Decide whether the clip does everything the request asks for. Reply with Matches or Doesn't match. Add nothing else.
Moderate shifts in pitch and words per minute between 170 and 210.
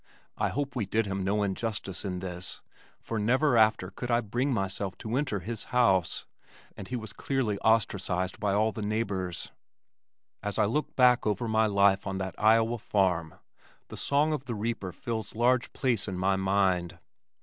Matches